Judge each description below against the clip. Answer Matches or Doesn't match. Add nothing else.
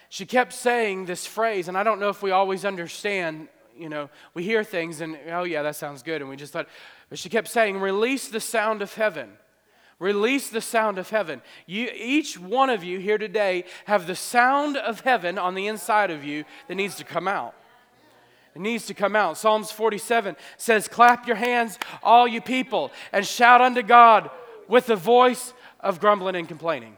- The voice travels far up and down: Doesn't match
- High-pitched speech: Matches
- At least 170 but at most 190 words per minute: Doesn't match